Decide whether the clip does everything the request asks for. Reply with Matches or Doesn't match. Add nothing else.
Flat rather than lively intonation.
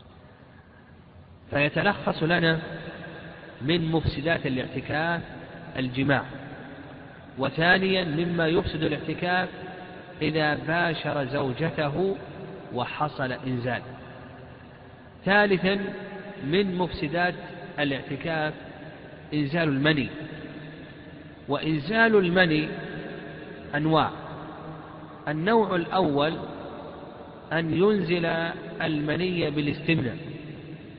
Doesn't match